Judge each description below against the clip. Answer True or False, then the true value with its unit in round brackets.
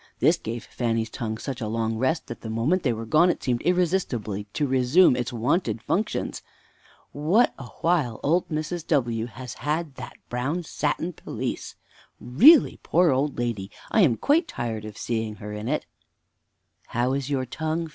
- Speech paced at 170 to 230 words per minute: True (180 wpm)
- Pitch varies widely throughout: True (6.1 semitones)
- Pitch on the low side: True (130 Hz)